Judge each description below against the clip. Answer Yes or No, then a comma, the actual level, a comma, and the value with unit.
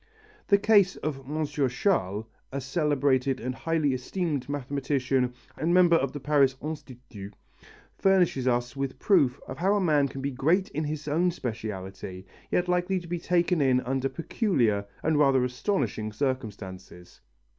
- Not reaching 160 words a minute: Yes, average, 150 wpm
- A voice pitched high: No, medium, 140 Hz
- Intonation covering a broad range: No, average, 4.9 semitones